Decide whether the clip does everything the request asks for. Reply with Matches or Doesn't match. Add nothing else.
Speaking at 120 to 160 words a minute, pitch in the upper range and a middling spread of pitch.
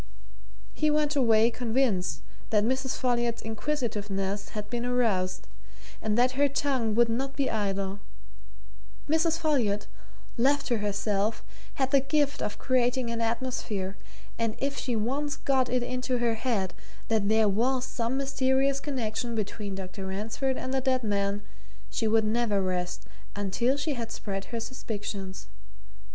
Matches